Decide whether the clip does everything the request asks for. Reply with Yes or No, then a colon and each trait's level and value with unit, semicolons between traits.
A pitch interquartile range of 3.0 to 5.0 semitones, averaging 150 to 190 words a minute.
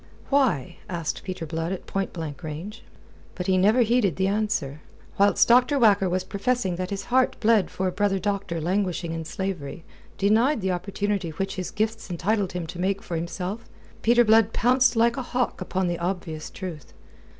Yes: average, 3.9 semitones; average, 180 wpm